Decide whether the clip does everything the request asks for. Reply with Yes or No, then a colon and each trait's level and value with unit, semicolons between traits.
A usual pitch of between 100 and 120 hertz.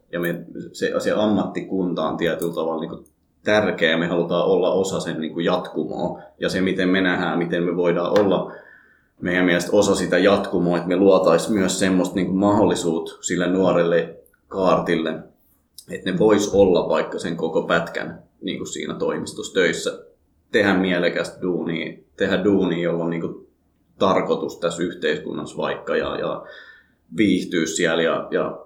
No: very low, 90 Hz